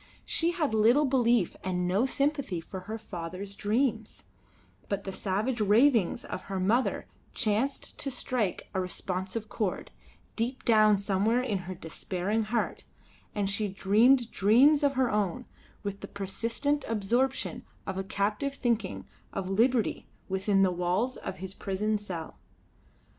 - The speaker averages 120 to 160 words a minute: Yes, average, 140 wpm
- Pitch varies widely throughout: No, average, 4.1 semitones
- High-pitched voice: Yes, high, 210 Hz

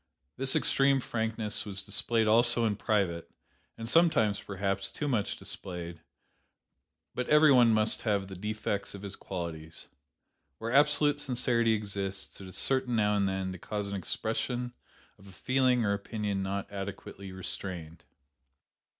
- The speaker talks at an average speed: Yes, average, 145 wpm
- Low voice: Yes, low, 105 Hz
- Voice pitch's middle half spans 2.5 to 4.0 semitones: Yes, average, 3.6 semitones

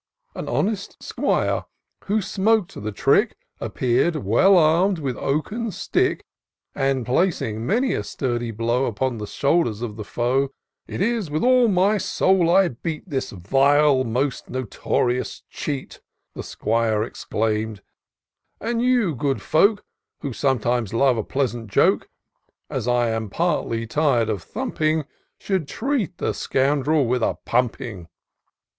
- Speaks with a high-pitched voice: No, low, 135 Hz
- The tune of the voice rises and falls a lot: Yes, wide, 7.4 semitones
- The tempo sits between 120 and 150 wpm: Yes, average, 140 wpm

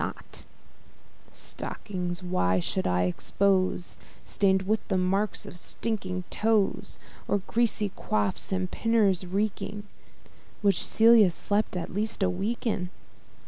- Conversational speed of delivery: No, slow, 120 wpm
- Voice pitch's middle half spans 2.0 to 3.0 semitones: Yes, average, 2.7 semitones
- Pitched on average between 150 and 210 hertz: Yes, high, 190 Hz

